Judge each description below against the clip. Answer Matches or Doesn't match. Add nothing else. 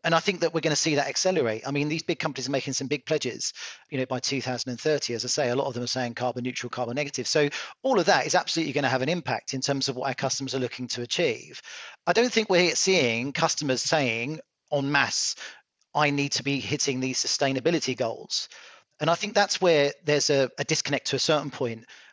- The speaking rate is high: Matches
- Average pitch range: Matches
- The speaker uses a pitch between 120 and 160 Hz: Matches